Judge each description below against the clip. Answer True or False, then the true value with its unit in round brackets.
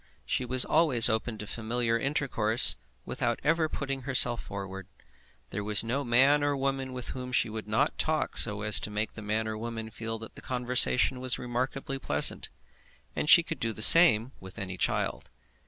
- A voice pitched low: True (120 Hz)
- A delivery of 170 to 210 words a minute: True (185 wpm)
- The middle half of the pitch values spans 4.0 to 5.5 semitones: False (3.5 semitones)